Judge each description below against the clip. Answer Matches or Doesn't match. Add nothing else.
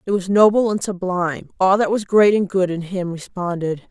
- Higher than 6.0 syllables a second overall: Doesn't match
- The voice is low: Doesn't match